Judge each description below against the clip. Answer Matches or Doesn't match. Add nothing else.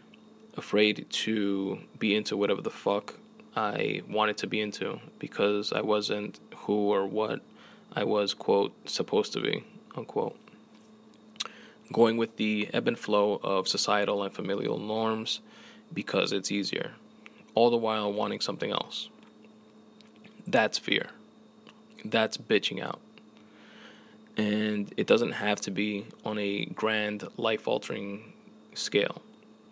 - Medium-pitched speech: Doesn't match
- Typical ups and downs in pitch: Doesn't match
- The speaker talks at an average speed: Doesn't match